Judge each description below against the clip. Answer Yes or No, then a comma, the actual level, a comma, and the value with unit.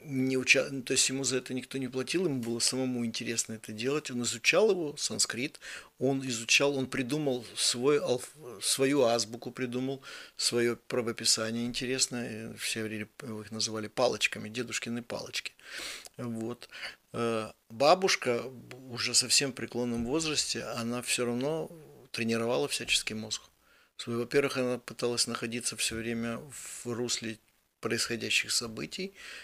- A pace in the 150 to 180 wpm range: No, average, 130 wpm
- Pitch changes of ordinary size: No, narrow, 2.3 semitones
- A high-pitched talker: No, low, 120 Hz